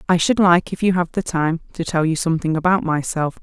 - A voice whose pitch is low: No, medium, 170 Hz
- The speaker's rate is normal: No, fast, 245 wpm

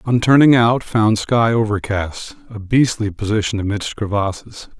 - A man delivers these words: Yes, male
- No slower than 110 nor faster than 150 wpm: Yes, average, 140 wpm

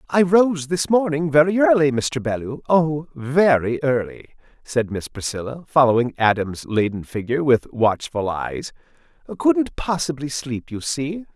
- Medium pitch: Yes, medium, 145 Hz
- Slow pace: Yes, slow, 125 wpm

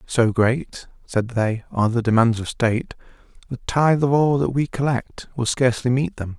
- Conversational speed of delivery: Yes, average, 190 wpm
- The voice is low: Yes, low, 125 Hz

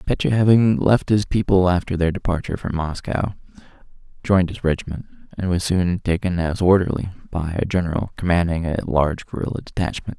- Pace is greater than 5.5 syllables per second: Yes, 5.8 syllables/s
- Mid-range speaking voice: No, very low, 90 Hz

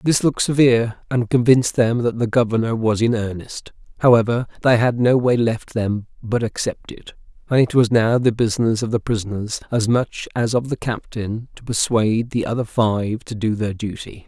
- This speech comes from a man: Yes, male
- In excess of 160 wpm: Yes, average, 195 wpm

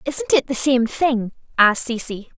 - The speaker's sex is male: No, female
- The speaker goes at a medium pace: Yes, average, 175 wpm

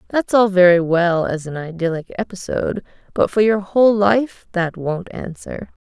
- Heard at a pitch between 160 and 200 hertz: Yes, high, 190 Hz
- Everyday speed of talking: Yes, average, 165 wpm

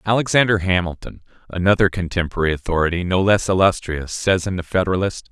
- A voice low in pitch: Yes, very low, 95 Hz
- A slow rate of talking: Yes, slow, 115 wpm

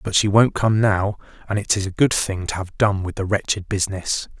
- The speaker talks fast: Yes, fast, 245 wpm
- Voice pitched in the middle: No, low, 100 Hz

